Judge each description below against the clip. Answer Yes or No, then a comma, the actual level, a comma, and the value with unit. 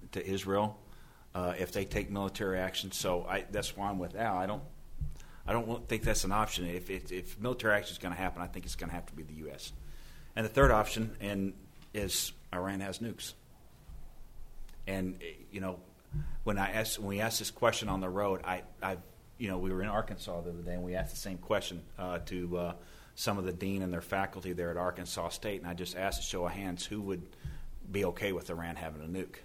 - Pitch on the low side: Yes, very low, 95 Hz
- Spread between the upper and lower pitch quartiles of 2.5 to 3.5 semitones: Yes, average, 2.8 semitones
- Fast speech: Yes, fast, 230 wpm